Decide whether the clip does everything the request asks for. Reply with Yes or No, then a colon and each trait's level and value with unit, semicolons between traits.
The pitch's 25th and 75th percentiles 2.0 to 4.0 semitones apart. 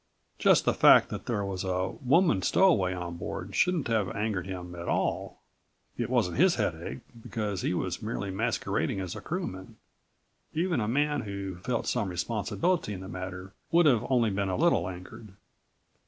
No: average, 4.9 semitones